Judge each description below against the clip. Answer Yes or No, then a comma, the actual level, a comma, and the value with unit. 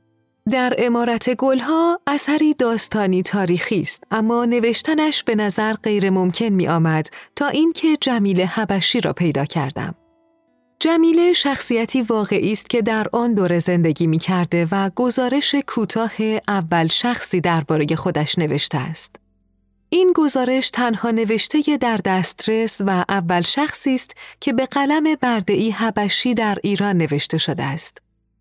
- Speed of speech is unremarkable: Yes, average, 130 wpm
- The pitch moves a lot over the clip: Yes, wide, 6.3 semitones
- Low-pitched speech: No, high, 220 Hz